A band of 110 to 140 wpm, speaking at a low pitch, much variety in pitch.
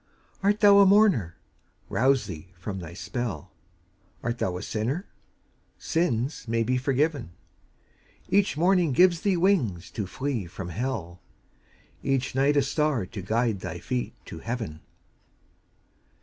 Yes: slow, 135 wpm; low, 125 Hz; wide, 8.2 semitones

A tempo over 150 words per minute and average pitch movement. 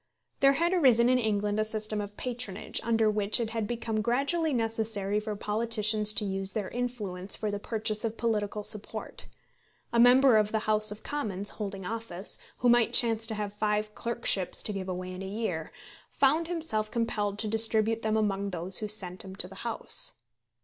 No: average, 185 wpm; narrow, 2.2 semitones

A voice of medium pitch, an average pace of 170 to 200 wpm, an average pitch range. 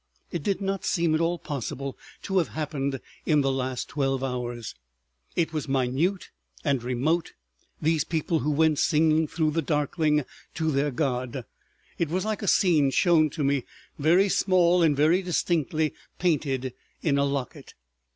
No: medium, 150 Hz; average, 160 wpm; average, 3.6 semitones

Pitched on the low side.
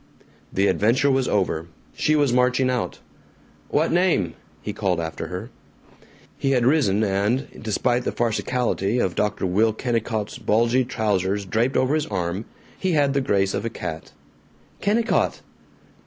Yes: low, 115 Hz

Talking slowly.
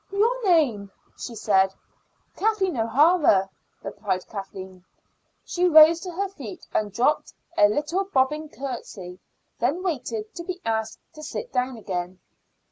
Yes: slow, 130 wpm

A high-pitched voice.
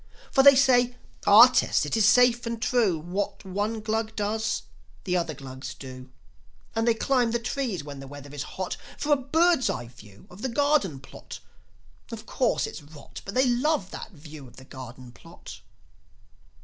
Yes: high, 205 Hz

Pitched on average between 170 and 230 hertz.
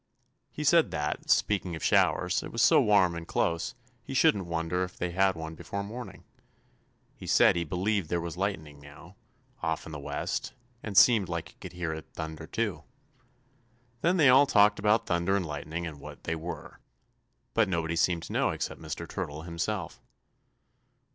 No: very low, 90 Hz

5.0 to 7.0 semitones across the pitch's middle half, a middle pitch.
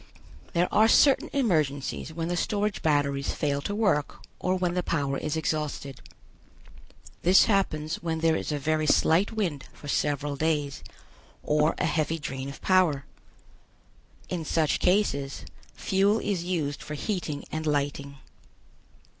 No: average, 4.0 semitones; medium, 155 Hz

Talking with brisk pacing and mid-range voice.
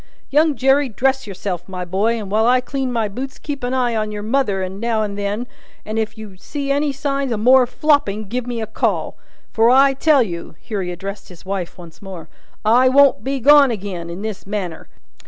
No: fast, 210 wpm; high, 220 Hz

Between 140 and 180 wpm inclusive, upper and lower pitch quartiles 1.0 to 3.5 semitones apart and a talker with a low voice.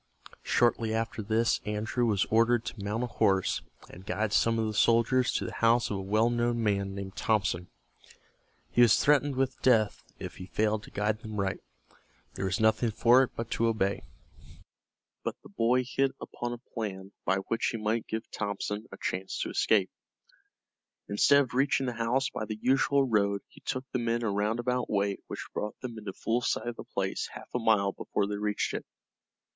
No: average, 195 wpm; average, 2.7 semitones; low, 110 Hz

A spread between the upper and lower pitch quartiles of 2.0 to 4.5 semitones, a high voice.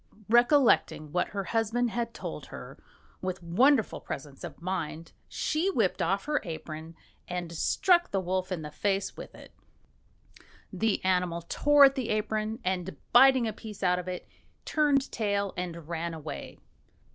No: wide, 5.5 semitones; high, 195 Hz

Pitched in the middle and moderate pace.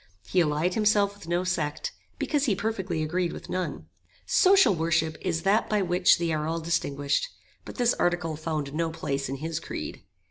Yes: medium, 170 Hz; average, 180 wpm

